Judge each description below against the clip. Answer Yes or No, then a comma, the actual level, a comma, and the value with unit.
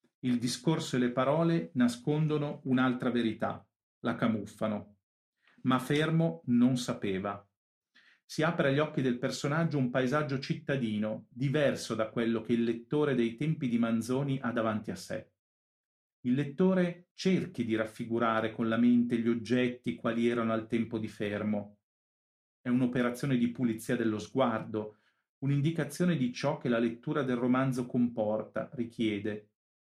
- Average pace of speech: Yes, average, 140 wpm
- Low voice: Yes, low, 125 Hz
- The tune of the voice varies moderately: Yes, average, 3.8 semitones